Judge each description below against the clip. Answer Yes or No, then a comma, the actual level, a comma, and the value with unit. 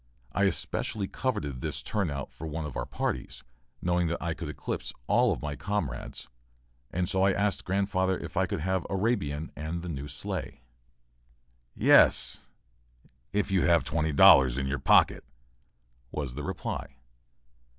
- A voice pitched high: No, very low, 85 Hz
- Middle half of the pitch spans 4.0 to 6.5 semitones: Yes, average, 4.6 semitones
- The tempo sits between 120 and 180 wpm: Yes, average, 150 wpm